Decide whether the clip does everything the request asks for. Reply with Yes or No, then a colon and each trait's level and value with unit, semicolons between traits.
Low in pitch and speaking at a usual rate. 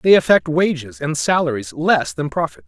No: medium, 145 Hz; average, 180 wpm